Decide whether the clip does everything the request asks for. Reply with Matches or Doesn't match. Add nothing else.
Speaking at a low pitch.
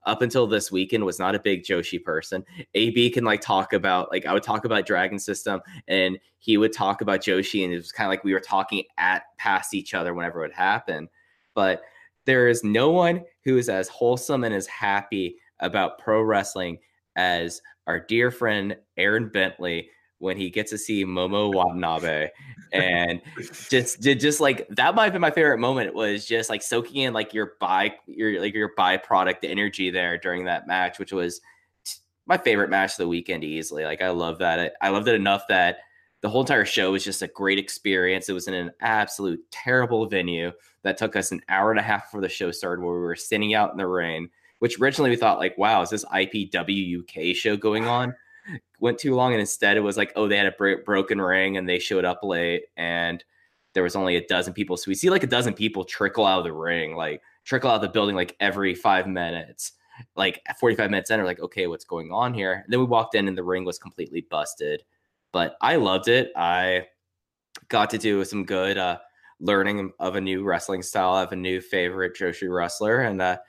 Matches